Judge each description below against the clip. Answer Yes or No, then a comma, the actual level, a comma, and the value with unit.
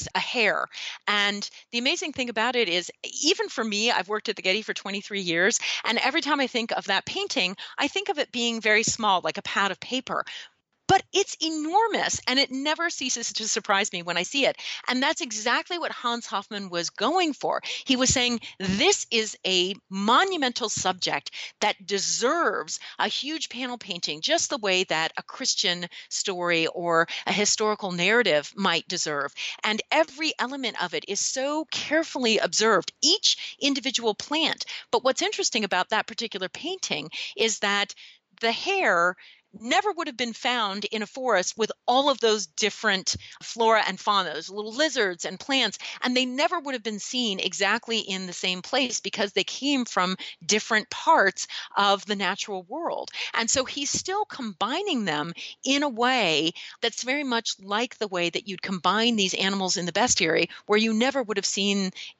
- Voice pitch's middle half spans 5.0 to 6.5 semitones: Yes, wide, 5.4 semitones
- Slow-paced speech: No, average, 180 wpm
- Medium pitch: No, high, 225 Hz